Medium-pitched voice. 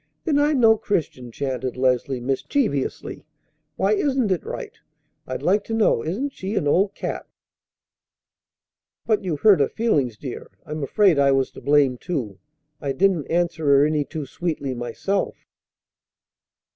Yes: medium, 155 Hz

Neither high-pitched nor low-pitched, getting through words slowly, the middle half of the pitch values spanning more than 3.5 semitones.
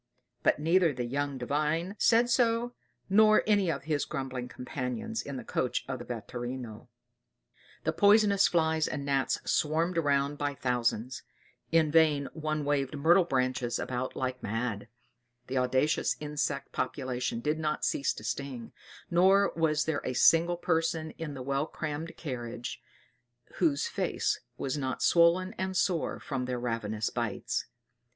No: medium, 145 Hz; average, 145 wpm; average, 4.6 semitones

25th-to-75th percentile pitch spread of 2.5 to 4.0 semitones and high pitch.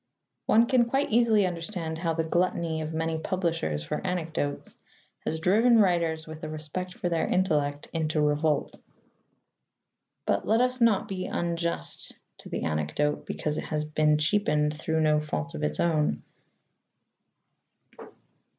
No: average, 3.2 semitones; medium, 160 Hz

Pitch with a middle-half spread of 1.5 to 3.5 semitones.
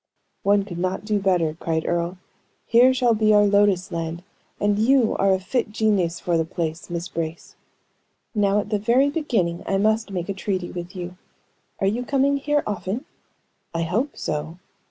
No: average, 3.9 semitones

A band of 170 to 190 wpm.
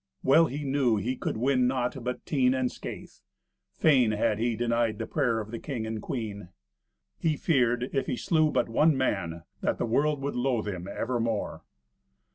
Yes: average, 180 wpm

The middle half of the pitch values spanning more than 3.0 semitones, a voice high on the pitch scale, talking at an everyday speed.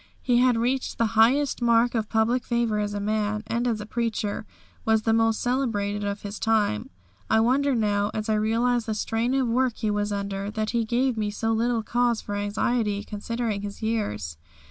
No: narrow, 2.4 semitones; high, 220 Hz; average, 195 wpm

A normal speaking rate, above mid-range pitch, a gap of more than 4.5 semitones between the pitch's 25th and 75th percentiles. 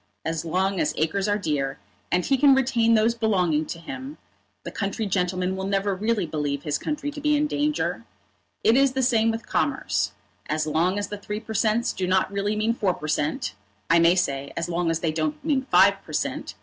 No: fast, 215 wpm; high, 195 Hz; wide, 5.6 semitones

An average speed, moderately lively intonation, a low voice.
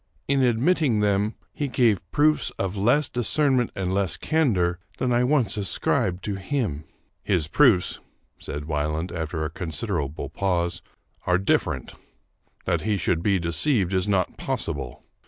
No: average, 150 wpm; wide, 6.0 semitones; very low, 95 Hz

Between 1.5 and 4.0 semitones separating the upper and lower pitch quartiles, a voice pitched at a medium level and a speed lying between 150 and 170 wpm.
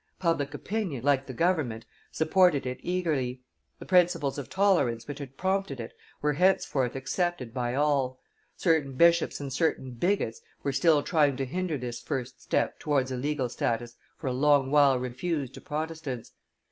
No: average, 4.6 semitones; medium, 145 Hz; average, 160 wpm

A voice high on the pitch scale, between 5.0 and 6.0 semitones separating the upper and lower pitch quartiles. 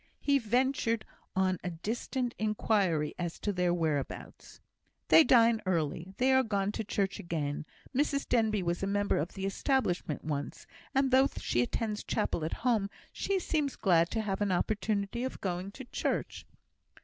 Yes: high, 205 Hz; average, 5.3 semitones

